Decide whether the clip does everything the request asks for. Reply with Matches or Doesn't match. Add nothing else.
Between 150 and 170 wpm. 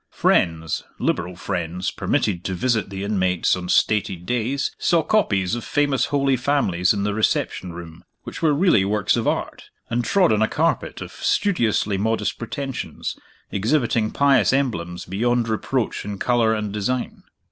Matches